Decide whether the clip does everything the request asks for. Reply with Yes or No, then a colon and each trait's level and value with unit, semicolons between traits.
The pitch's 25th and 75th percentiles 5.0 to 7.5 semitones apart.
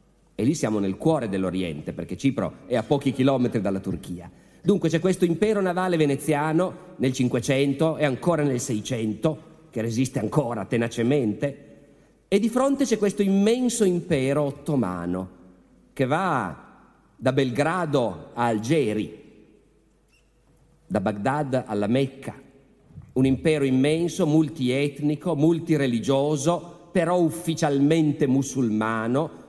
Yes: average, 5.3 semitones